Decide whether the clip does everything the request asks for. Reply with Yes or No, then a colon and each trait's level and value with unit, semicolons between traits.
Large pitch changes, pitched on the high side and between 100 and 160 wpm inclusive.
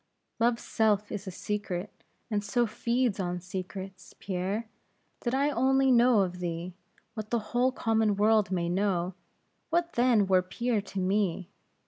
No: average, 4.1 semitones; high, 210 Hz; average, 150 wpm